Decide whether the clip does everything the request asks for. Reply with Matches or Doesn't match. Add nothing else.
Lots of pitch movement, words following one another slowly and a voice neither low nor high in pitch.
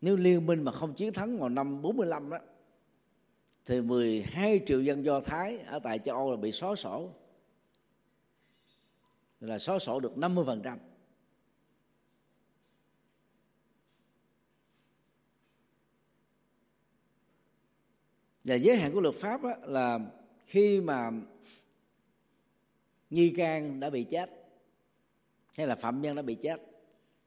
Matches